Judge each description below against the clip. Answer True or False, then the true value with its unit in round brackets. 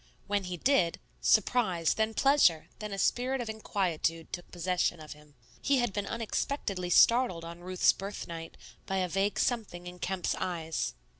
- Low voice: False (185 Hz)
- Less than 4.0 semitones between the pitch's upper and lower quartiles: False (4.3 semitones)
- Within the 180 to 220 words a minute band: False (160 wpm)